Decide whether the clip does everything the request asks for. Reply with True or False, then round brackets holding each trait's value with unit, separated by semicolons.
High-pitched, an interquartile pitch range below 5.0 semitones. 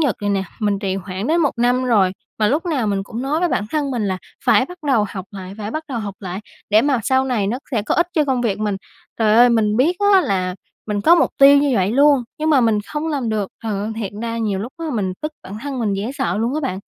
False (230 Hz; 5.6 semitones)